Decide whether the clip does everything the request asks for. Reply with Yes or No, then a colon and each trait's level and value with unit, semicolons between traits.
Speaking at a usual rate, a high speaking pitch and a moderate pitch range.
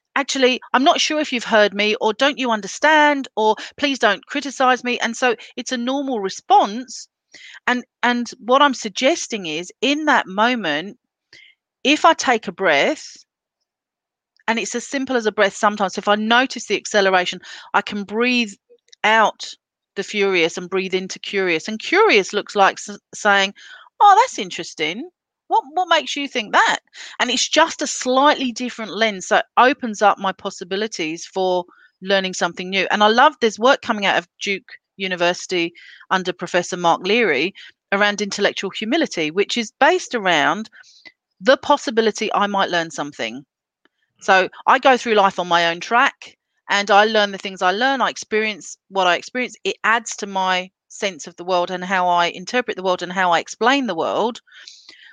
Yes: average, 175 wpm; high, 215 Hz; average, 5.0 semitones